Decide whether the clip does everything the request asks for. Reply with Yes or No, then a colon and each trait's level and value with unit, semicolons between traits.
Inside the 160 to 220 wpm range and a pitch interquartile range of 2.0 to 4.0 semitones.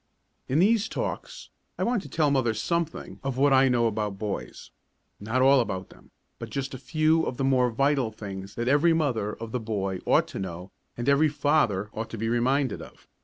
No: fast, 205 wpm; average, 4.7 semitones